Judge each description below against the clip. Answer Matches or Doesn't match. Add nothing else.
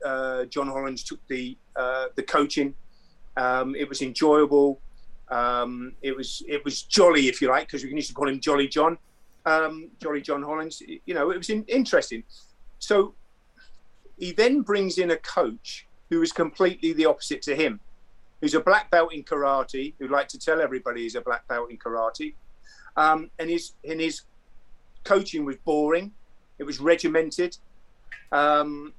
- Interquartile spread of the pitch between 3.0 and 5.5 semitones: Matches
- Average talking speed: Matches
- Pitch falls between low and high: Matches